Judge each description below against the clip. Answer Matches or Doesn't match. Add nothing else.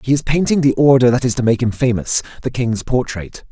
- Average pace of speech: Doesn't match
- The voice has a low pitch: Matches